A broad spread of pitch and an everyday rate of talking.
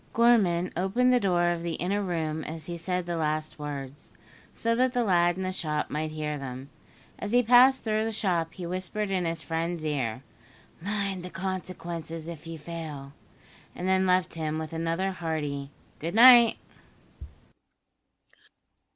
No: average, 3.5 semitones; average, 160 wpm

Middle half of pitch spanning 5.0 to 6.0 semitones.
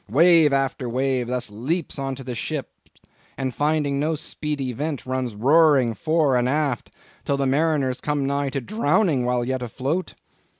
No: average, 3.0 semitones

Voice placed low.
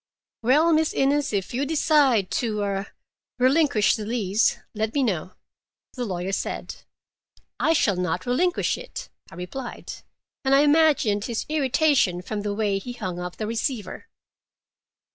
No: high, 235 Hz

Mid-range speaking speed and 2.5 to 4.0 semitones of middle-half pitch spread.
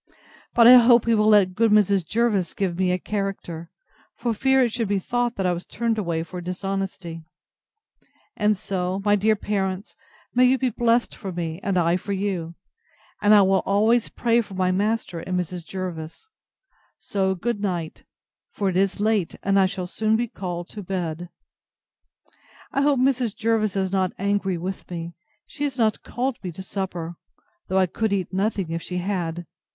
Yes: average, 185 wpm; average, 3.4 semitones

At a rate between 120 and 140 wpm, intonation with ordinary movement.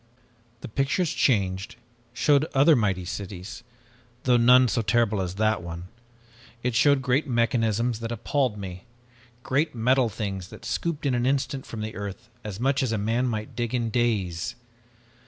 No: average, 160 wpm; average, 3.9 semitones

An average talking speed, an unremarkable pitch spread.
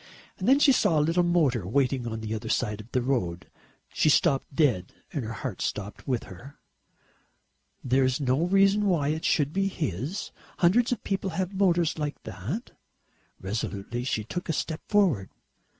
No: average, 175 wpm; wide, 7.5 semitones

